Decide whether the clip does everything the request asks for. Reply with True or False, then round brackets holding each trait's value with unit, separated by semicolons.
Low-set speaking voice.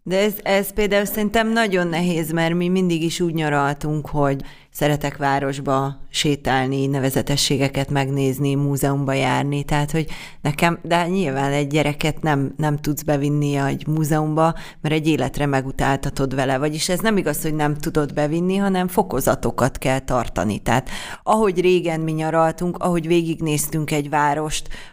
False (150 Hz)